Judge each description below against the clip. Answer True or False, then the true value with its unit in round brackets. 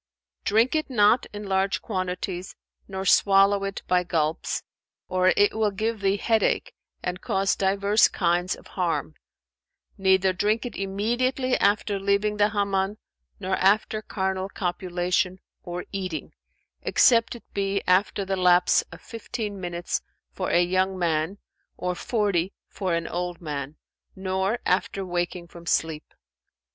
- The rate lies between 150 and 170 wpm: False (140 wpm)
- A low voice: False (190 Hz)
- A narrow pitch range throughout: True (2.3 semitones)